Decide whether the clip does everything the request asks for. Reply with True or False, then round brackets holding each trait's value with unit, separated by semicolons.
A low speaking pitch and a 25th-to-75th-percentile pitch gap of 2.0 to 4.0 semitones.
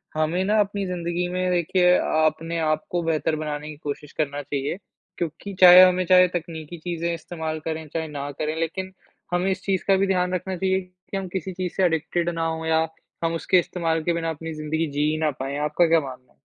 False (165 Hz; 2.6 semitones)